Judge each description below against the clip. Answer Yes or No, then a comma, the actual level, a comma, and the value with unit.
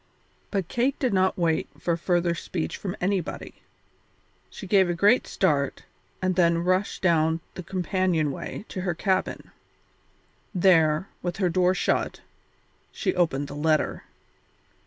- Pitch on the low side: No, medium, 180 Hz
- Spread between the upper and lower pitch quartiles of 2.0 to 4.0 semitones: Yes, narrow, 2.4 semitones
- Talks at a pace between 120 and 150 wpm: Yes, slow, 135 wpm